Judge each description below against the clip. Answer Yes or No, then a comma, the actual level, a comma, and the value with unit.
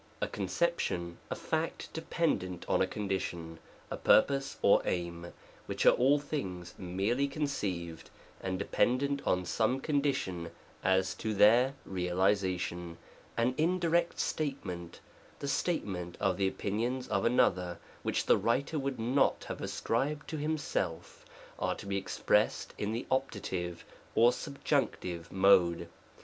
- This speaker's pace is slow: Yes, slow, 130 wpm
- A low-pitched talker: Yes, low, 105 Hz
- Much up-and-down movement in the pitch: Yes, wide, 7.4 semitones